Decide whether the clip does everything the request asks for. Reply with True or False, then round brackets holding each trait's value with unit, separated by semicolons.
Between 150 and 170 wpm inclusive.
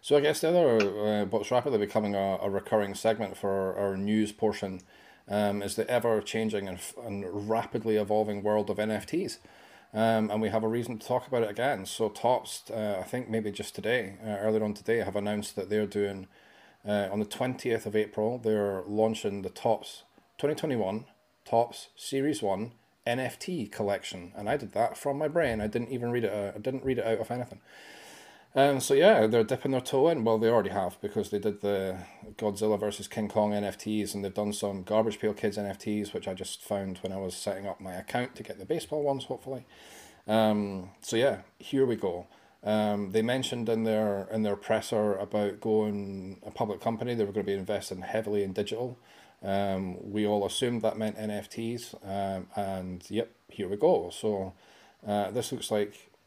False (200 wpm)